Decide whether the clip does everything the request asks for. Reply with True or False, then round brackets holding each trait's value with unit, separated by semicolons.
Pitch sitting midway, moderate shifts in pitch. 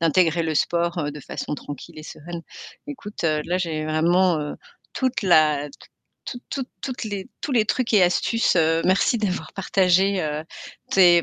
True (175 Hz; 3.9 semitones)